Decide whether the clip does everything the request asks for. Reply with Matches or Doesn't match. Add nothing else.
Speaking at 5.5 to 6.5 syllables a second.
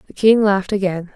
Matches